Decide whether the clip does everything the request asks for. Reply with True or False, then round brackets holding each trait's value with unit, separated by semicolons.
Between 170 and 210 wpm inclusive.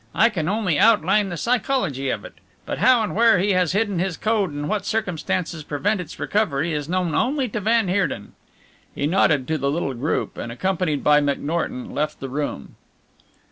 True (185 wpm)